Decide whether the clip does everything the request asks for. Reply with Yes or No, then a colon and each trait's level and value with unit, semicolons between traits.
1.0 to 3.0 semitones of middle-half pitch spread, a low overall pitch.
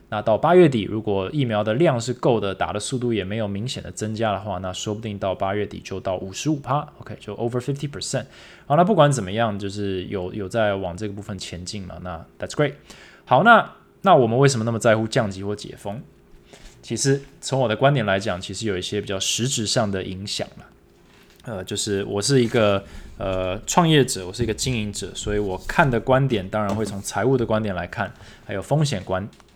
No: average, 4.1 semitones; low, 105 Hz